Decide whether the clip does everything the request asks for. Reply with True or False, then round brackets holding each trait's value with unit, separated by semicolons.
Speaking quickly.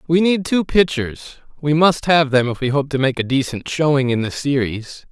True (210 wpm)